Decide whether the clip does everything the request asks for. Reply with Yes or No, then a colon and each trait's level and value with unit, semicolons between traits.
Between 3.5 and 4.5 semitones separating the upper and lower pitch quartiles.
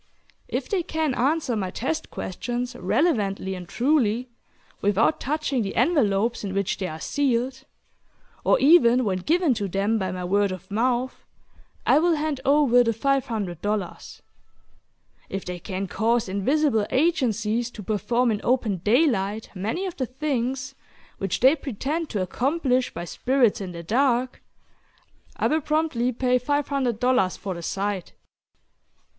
No: wide, 5.5 semitones